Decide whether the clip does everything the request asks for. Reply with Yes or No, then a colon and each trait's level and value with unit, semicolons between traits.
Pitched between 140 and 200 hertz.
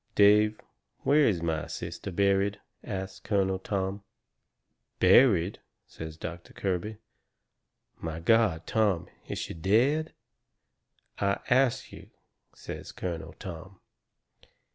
No: very low, 95 Hz